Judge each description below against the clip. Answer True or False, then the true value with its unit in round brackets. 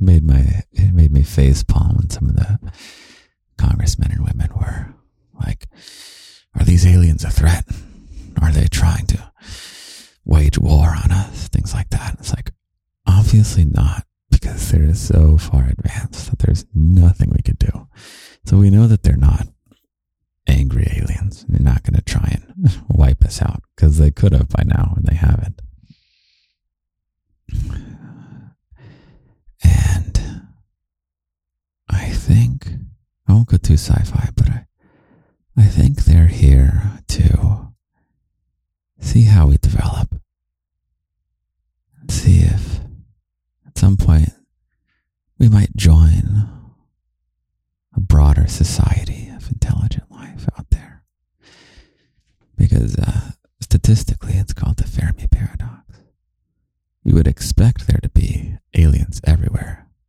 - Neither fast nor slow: False (125 wpm)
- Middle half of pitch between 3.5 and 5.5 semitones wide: True (4.5 semitones)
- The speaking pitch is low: True (90 Hz)